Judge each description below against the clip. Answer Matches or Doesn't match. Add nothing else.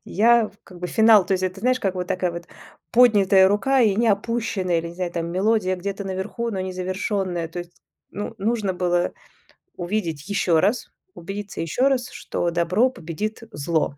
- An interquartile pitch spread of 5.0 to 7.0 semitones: Doesn't match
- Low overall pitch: Doesn't match